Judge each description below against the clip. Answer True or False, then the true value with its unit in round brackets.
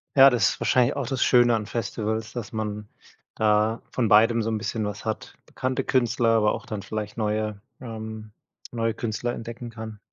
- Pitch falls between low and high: False (110 Hz)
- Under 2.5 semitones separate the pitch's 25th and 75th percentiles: True (1.9 semitones)